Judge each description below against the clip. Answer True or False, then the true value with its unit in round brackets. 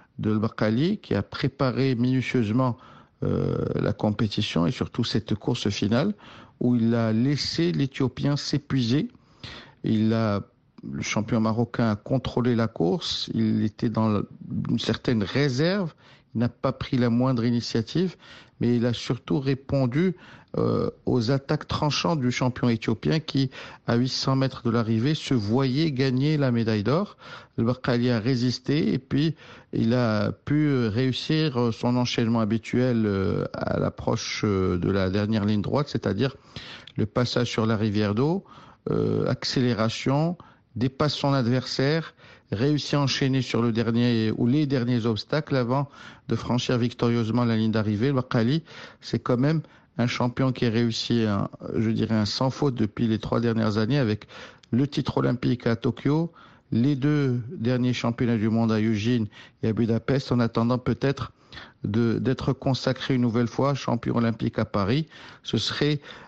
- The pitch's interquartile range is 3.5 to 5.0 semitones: False (3.0 semitones)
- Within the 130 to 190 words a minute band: True (150 wpm)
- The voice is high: False (125 Hz)